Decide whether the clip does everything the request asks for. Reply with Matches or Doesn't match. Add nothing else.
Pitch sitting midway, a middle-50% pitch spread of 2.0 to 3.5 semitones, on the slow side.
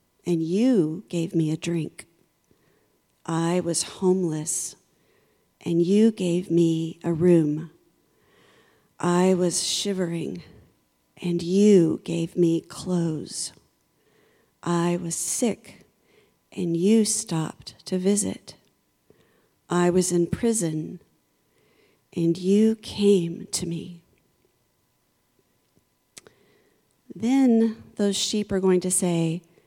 Matches